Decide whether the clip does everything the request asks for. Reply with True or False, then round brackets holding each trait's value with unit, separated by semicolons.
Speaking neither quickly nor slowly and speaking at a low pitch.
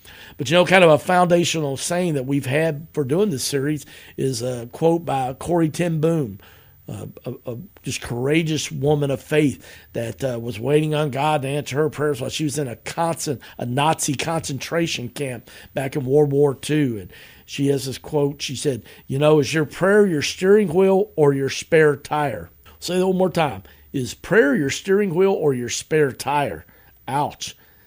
False (195 wpm; 145 Hz)